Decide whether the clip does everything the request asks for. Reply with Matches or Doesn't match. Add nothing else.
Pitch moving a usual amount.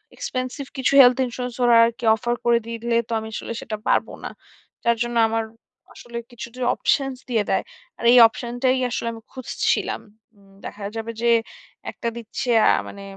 Doesn't match